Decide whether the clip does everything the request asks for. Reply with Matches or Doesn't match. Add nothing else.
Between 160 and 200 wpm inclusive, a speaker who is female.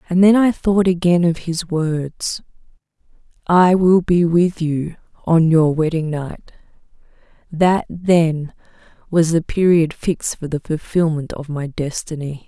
Doesn't match